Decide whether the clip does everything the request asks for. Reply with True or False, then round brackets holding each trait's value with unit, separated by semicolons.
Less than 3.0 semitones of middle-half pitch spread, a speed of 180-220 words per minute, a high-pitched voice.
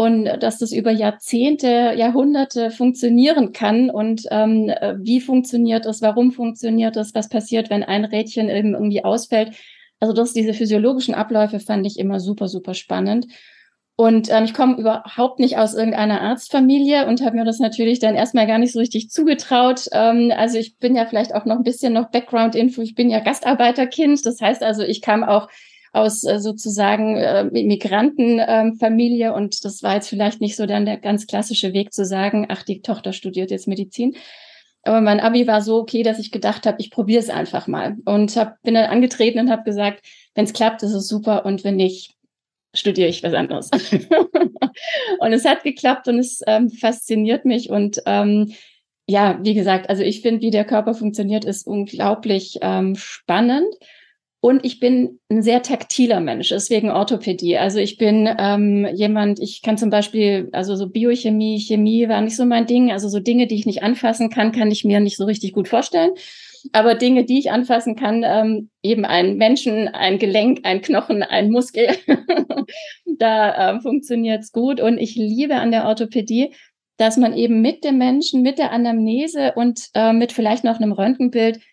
True (2.5 semitones; 185 wpm; 225 Hz)